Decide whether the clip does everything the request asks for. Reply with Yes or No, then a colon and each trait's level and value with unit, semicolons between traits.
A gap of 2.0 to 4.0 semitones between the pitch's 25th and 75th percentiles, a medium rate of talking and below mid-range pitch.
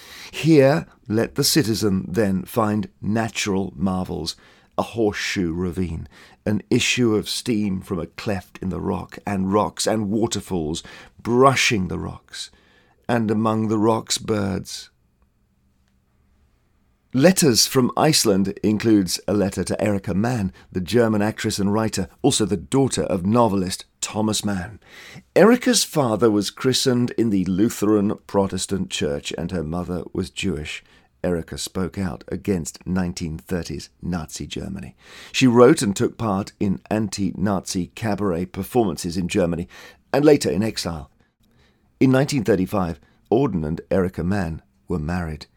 No: average, 3.7 semitones; slow, 130 wpm; low, 100 Hz